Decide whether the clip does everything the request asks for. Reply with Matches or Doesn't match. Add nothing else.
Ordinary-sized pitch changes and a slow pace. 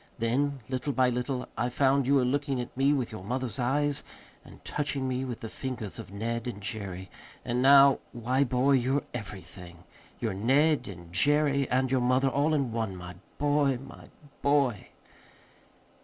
Doesn't match